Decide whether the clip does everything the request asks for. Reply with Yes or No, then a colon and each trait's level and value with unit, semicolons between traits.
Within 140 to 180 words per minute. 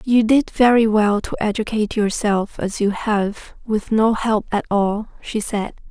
Yes: average, 175 wpm